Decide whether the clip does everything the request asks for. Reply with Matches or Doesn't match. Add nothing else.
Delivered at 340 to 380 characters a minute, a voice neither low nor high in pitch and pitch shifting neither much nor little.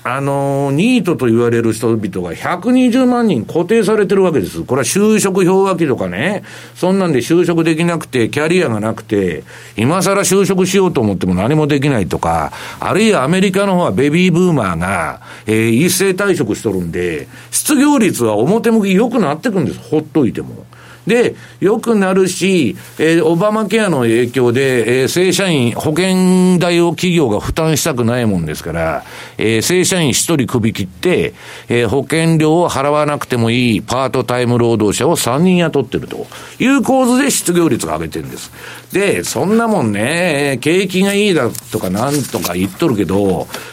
Doesn't match